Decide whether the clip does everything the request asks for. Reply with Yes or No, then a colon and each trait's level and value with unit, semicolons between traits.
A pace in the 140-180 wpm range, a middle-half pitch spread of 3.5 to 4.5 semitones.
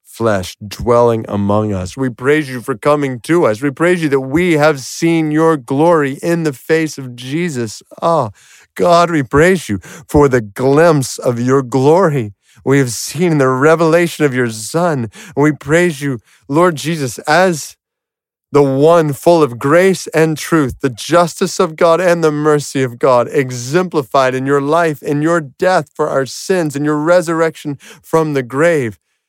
Yes: average, 170 wpm; average, 4.2 semitones